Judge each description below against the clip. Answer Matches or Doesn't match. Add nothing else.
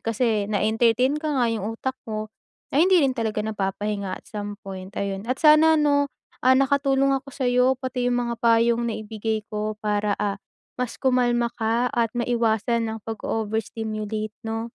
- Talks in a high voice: Matches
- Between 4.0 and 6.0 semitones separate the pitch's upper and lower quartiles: Doesn't match